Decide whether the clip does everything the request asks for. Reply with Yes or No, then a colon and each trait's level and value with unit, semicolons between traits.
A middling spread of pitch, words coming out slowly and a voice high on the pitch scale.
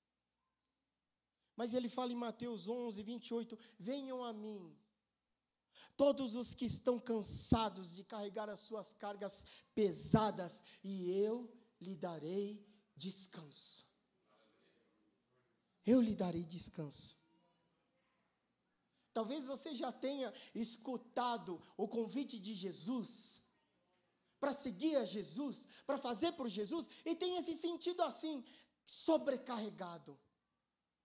Yes: average, 4.3 semitones; slow, 100 wpm; high, 230 Hz